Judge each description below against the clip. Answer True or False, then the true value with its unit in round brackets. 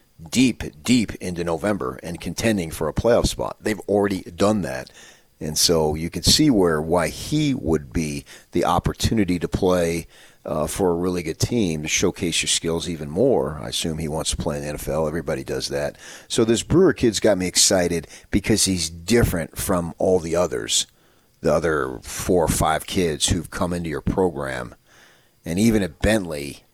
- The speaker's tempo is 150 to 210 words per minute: True (180 wpm)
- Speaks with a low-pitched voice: True (90 Hz)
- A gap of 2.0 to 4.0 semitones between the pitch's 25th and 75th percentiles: False (4.4 semitones)